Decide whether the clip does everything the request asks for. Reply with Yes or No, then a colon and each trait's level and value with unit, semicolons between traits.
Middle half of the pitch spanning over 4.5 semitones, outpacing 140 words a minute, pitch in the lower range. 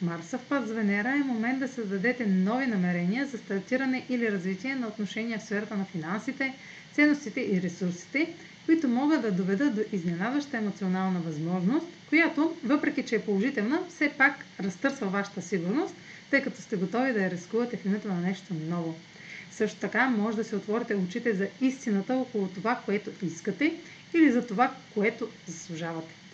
No: average, 5.3 semitones; average, 160 wpm; high, 215 Hz